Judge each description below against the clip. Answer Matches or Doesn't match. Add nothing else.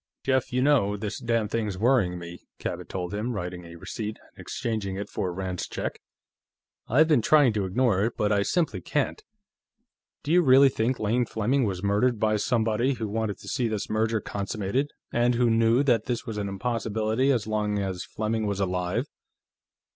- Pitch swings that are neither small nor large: Matches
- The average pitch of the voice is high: Doesn't match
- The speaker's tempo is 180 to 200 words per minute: Matches